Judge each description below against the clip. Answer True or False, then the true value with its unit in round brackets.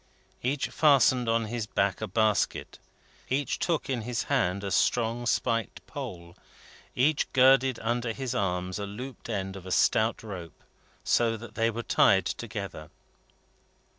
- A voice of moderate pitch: False (115 Hz)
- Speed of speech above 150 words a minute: False (145 wpm)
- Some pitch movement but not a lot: True (3.9 semitones)